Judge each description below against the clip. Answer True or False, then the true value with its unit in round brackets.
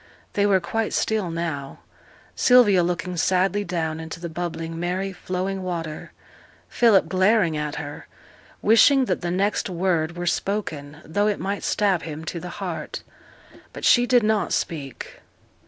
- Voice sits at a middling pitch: True (180 Hz)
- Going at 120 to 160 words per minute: True (150 wpm)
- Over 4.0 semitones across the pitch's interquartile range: False (3.6 semitones)